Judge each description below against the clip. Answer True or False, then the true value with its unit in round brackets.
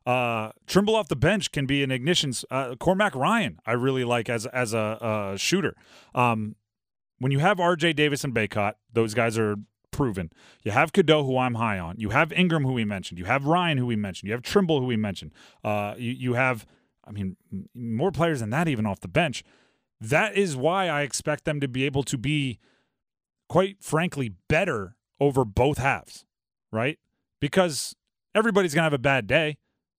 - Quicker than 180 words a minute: True (195 wpm)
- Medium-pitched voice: False (130 Hz)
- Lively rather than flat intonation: True (6.1 semitones)